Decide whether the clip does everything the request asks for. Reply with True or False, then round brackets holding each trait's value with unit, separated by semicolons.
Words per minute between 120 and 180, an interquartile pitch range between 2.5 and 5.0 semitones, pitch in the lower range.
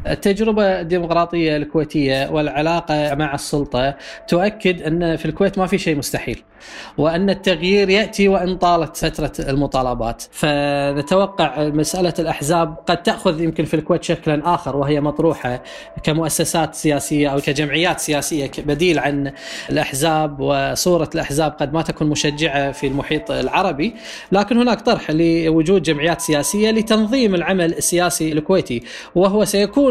False (125 wpm; 3.4 semitones; 160 Hz)